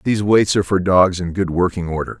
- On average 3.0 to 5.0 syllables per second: No, 6.3 syllables/s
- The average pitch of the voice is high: No, very low, 95 Hz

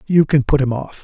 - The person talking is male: Yes, male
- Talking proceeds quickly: Yes, fast, 290 wpm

